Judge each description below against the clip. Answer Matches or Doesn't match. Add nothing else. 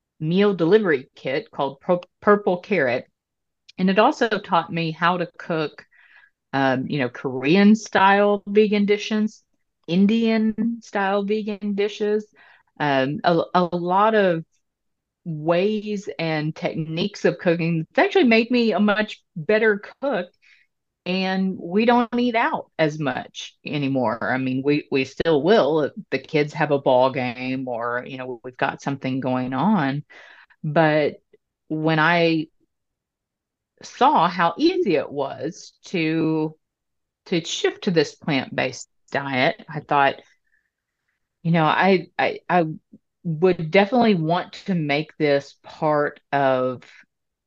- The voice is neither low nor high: Matches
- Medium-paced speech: Doesn't match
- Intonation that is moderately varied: Doesn't match